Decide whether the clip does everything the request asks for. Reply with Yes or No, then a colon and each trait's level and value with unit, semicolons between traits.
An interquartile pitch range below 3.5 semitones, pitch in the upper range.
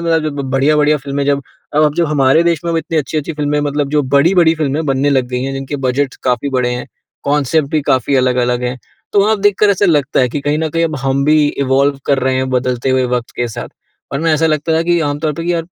No: average, 2.9 semitones; medium, 145 Hz